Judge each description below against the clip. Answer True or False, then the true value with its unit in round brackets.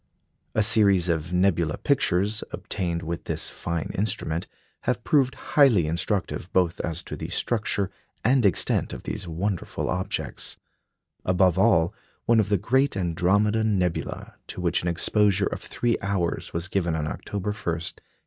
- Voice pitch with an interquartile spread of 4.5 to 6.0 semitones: False (3.8 semitones)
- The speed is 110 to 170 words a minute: True (150 wpm)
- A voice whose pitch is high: False (95 Hz)